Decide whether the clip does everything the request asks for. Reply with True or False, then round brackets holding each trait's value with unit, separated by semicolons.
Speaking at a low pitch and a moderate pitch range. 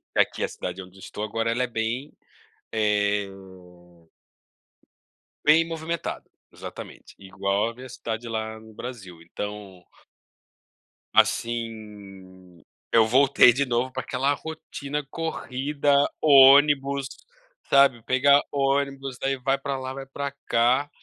True (125 Hz; 4.4 semitones)